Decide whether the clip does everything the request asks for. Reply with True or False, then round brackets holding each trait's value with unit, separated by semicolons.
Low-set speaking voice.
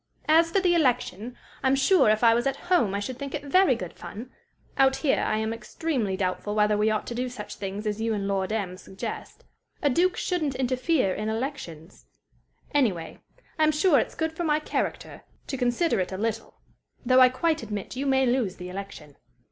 False (245 Hz)